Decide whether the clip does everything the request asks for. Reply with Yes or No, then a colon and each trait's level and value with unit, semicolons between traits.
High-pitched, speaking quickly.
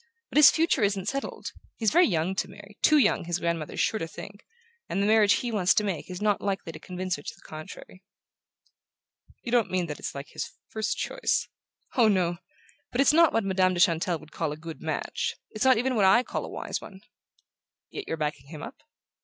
Yes: high, 195 Hz; fast, 220 wpm